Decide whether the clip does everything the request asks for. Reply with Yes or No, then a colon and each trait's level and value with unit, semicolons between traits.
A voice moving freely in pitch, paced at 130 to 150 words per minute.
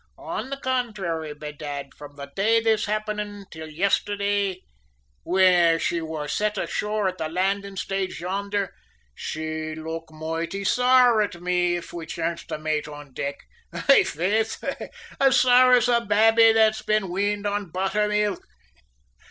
No: average, 4.6 semitones; average, 145 wpm